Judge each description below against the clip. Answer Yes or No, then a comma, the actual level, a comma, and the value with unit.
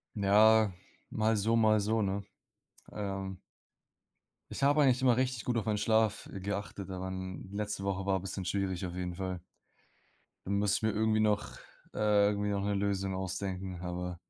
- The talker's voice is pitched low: Yes, low, 100 Hz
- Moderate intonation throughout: No, narrow, 2.3 semitones